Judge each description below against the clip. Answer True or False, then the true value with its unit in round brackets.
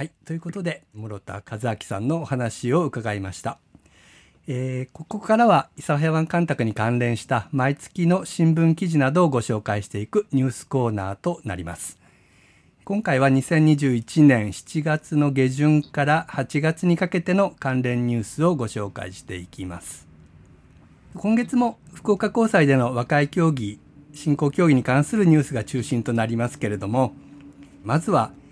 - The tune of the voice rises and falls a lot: True (5.9 semitones)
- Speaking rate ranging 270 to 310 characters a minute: True (300 characters per minute)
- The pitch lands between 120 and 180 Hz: True (140 Hz)